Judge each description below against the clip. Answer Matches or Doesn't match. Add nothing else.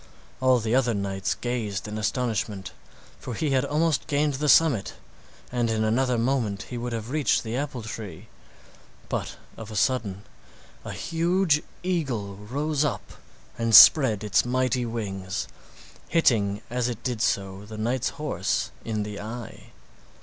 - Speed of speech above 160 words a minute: Doesn't match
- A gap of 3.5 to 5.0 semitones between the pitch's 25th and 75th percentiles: Matches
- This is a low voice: Matches